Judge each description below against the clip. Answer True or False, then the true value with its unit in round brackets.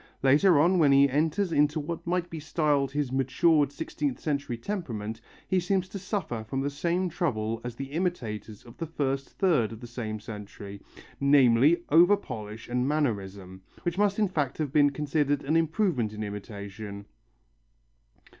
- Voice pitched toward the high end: False (140 Hz)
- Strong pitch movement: True (6.3 semitones)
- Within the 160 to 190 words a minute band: True (165 wpm)